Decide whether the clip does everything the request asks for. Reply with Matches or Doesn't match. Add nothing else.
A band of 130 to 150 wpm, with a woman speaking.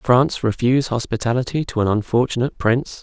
Doesn't match